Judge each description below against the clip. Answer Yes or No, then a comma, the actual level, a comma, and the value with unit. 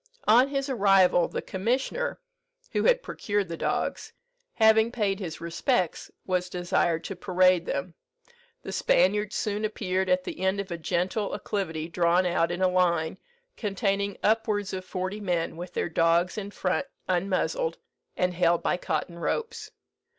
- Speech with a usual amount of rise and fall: Yes, average, 3.0 semitones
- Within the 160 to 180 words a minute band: No, average, 150 wpm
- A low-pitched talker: No, medium, 185 Hz